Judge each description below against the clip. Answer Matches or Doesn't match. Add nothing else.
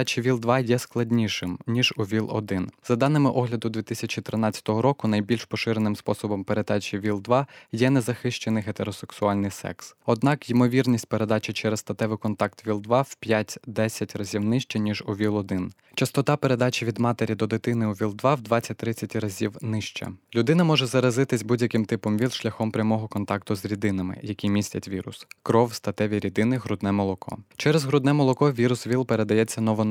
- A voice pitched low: Matches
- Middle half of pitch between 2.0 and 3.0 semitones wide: Matches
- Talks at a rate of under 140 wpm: Doesn't match